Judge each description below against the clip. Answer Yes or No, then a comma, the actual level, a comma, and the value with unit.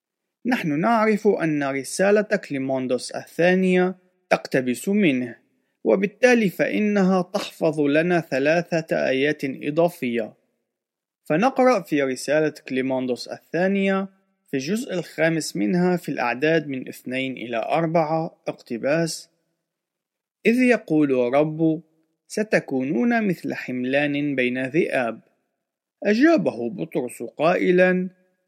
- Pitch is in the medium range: Yes, medium, 165 Hz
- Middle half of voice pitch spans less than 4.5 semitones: No, average, 5.1 semitones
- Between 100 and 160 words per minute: No, average, 90 wpm